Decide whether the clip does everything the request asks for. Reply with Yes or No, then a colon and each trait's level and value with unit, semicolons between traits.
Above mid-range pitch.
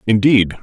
No: low, 110 Hz